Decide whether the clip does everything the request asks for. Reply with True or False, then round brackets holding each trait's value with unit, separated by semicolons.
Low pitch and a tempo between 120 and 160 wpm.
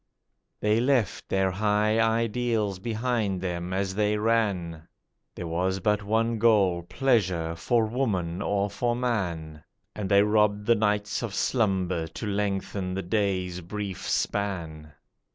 True (100 Hz; 135 wpm)